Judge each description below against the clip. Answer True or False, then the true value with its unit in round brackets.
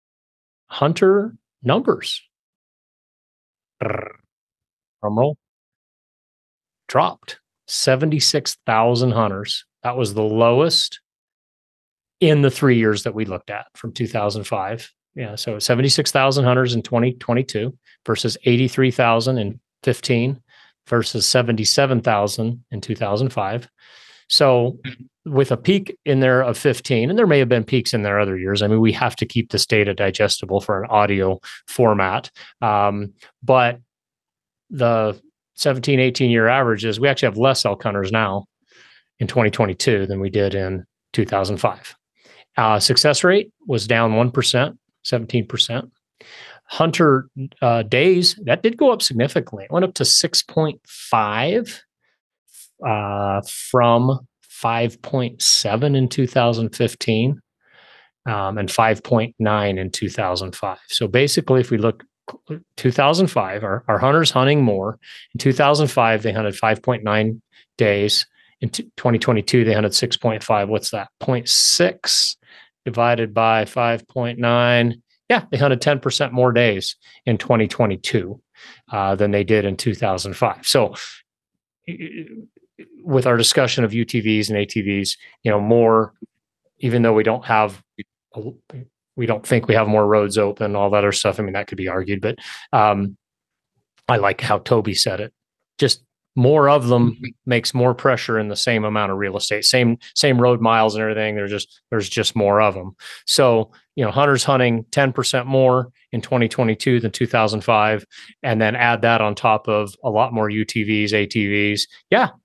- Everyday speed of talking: True (145 wpm)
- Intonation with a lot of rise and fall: False (3.3 semitones)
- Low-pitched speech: True (115 Hz)